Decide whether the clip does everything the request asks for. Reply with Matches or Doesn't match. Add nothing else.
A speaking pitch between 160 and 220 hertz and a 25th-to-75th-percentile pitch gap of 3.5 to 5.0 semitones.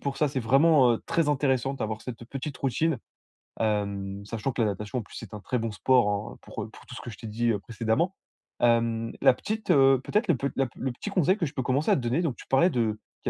Doesn't match